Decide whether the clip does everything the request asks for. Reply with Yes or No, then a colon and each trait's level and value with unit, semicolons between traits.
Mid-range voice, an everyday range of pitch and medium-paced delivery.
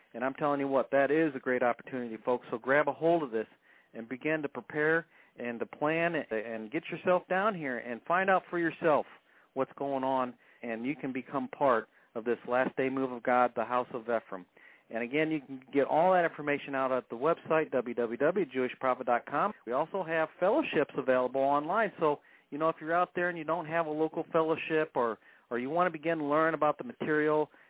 No: medium, 145 Hz; average, 4.2 semitones; fast, 210 wpm